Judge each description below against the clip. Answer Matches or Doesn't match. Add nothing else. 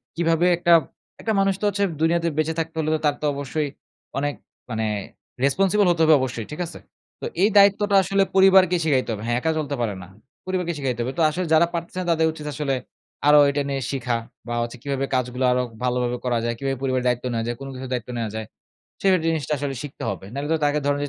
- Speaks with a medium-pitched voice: Matches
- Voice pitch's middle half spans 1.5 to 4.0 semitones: Doesn't match